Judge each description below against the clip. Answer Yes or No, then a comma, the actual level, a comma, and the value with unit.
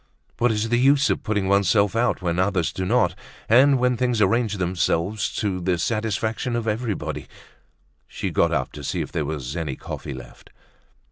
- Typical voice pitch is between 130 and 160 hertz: No, low, 105 Hz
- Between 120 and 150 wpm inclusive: No, average, 185 wpm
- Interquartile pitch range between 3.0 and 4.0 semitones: No, average, 4.5 semitones